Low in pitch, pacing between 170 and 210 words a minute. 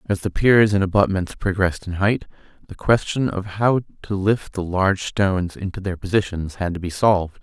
Yes: very low, 95 Hz; average, 195 wpm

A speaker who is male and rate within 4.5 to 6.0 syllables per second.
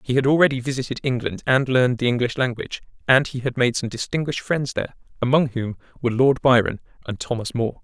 No: male; 6.6 syllables/s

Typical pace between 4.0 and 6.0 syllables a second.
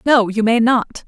Yes: 4.3 syllables/s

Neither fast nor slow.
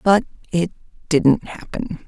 No: slow, 115 wpm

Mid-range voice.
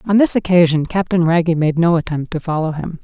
Yes: medium, 170 Hz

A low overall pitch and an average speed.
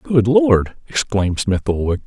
Yes: low, 105 Hz; average, 145 wpm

